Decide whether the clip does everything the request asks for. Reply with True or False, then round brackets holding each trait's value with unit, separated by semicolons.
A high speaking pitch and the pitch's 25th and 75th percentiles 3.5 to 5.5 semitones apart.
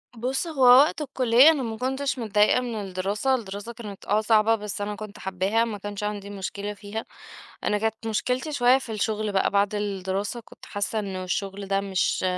False (210 Hz; 3.0 semitones)